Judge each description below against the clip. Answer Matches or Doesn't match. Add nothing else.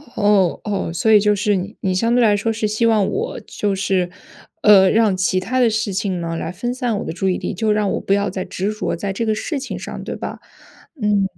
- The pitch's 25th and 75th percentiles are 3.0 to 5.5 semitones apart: Doesn't match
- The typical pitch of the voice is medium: Doesn't match